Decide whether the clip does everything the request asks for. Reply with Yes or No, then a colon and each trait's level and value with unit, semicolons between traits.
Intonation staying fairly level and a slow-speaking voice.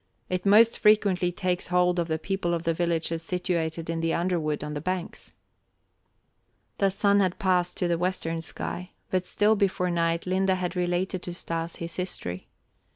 No: narrow, 1.9 semitones; average, 170 wpm